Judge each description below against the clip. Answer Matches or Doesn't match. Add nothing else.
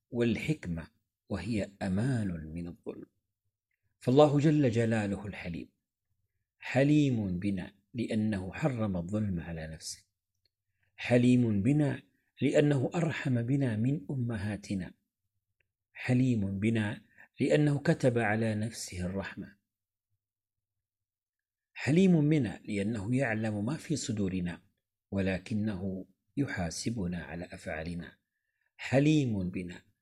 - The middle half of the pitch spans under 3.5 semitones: Doesn't match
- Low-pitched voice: Matches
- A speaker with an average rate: Matches